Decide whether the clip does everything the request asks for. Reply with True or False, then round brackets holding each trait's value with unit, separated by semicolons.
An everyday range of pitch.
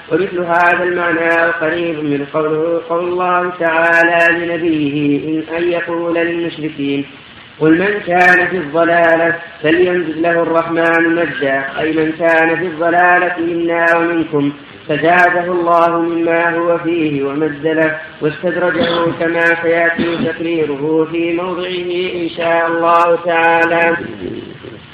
False (1.2 semitones)